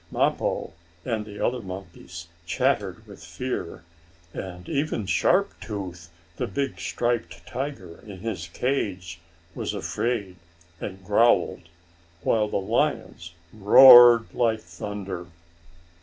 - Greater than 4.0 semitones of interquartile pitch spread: Yes, average, 4.9 semitones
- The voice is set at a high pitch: No, low, 100 Hz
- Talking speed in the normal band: No, slow, 110 wpm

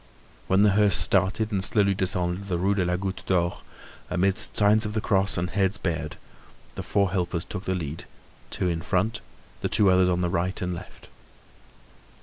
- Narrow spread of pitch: Yes, narrow, 2.2 semitones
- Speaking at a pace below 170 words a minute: No, average, 185 wpm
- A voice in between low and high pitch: No, very low, 95 Hz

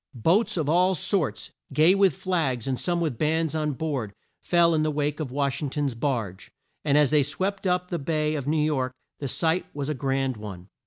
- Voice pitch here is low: No, medium, 150 Hz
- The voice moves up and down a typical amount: Yes, average, 3.5 semitones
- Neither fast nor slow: No, fast, 210 wpm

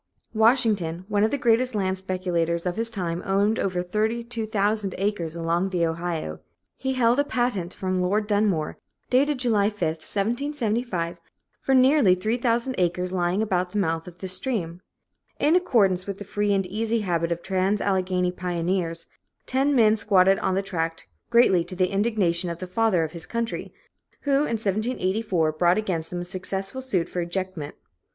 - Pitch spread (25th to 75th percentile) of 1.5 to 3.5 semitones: No, average, 4.0 semitones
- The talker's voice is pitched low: No, high, 195 Hz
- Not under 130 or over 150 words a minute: No, average, 165 wpm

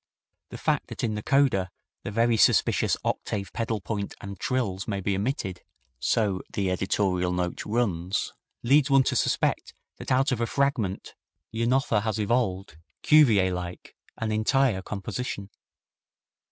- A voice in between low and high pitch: No, low, 105 Hz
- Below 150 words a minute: Yes, average, 140 wpm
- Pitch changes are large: No, average, 4.1 semitones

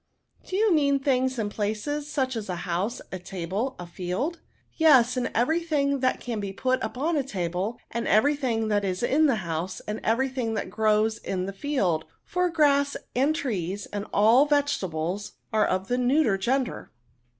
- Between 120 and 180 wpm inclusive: No, average, 190 wpm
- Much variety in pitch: Yes, wide, 6.0 semitones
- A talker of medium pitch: No, high, 235 Hz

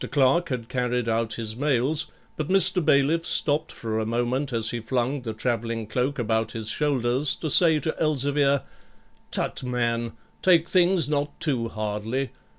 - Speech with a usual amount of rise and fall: Yes, average, 4.2 semitones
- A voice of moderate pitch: No, low, 130 Hz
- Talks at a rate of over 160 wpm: No, average, 155 wpm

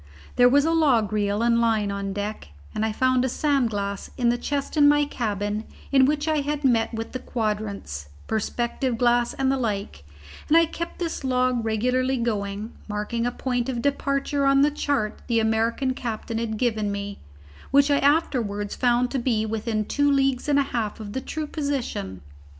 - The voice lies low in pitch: No, high, 240 Hz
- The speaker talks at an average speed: Yes, average, 190 wpm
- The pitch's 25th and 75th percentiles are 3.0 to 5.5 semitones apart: Yes, average, 4.3 semitones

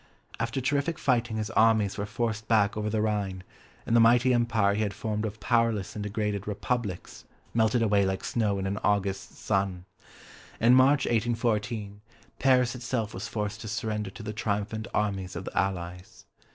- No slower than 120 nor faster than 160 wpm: No, average, 170 wpm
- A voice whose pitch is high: No, low, 110 Hz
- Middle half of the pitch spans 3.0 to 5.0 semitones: No, narrow, 2.4 semitones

